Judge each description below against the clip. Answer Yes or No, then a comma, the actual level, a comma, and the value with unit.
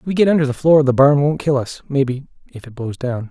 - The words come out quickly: Yes, fast, 290 wpm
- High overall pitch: No, medium, 140 Hz